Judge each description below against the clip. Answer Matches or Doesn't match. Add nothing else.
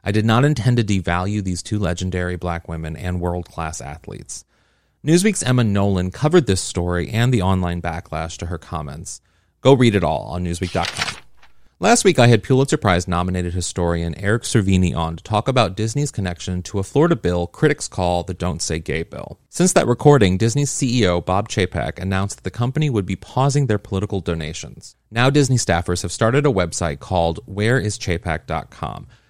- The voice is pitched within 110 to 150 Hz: Doesn't match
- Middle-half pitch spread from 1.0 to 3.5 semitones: Doesn't match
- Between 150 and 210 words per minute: Matches